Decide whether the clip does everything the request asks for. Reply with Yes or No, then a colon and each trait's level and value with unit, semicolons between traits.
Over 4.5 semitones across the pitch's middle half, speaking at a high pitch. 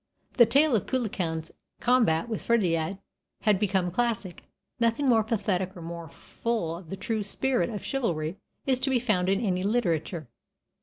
Yes: average, 5.1 semitones; high, 205 Hz